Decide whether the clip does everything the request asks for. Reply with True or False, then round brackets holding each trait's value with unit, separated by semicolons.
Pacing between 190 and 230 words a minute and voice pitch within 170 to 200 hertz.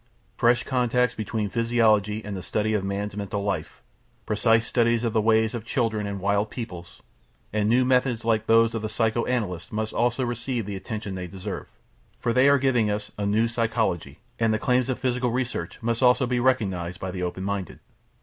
False (195 wpm; 110 Hz)